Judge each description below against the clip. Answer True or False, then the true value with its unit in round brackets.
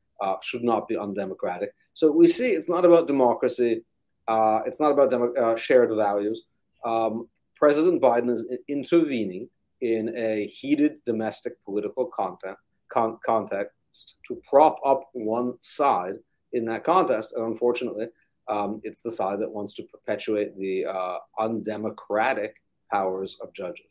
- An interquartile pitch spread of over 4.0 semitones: True (4.4 semitones)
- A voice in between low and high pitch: False (120 Hz)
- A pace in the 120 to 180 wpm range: True (145 wpm)